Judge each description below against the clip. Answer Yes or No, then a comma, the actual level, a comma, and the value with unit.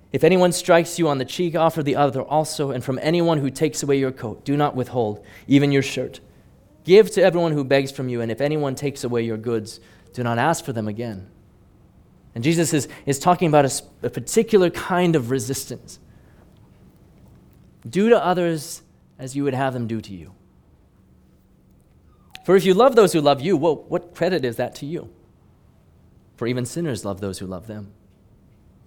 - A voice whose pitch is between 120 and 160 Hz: Yes, low, 135 Hz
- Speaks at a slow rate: No, average, 190 wpm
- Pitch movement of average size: No, wide, 7.2 semitones